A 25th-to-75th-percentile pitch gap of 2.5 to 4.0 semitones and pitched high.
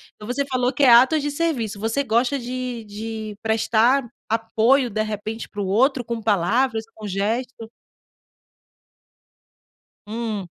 Yes: average, 2.8 semitones; high, 230 Hz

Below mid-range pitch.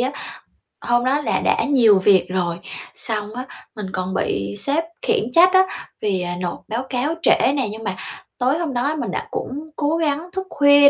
No: very high, 250 Hz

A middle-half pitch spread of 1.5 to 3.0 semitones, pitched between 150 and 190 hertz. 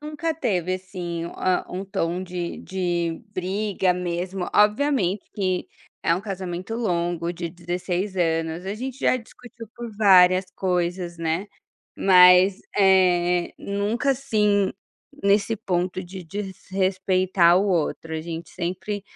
Yes: narrow, 2.5 semitones; medium, 185 Hz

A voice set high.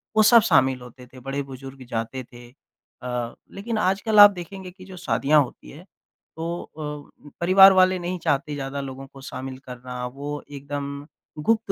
No: medium, 145 Hz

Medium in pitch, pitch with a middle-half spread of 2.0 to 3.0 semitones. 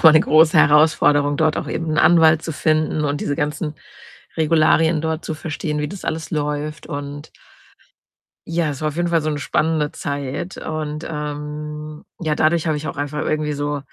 No: medium, 155 Hz; narrow, 1.3 semitones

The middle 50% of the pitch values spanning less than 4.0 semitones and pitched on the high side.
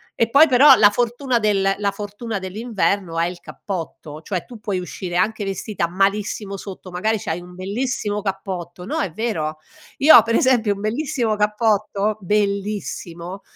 Yes: average, 3.0 semitones; high, 205 Hz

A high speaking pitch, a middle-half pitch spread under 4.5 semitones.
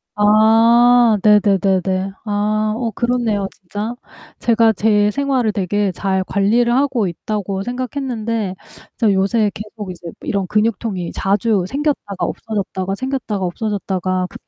Yes: high, 210 Hz; average, 2.9 semitones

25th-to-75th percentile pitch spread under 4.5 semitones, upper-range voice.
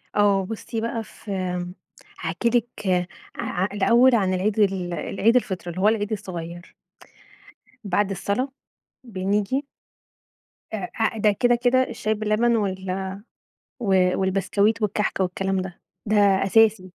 Yes: average, 2.9 semitones; high, 205 Hz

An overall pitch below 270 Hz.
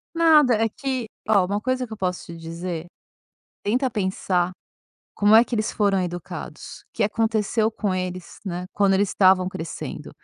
Yes: high, 200 Hz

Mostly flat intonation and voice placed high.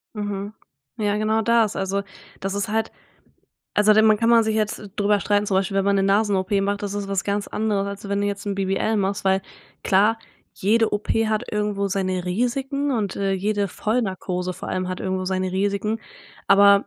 Yes: narrow, 1.7 semitones; high, 200 Hz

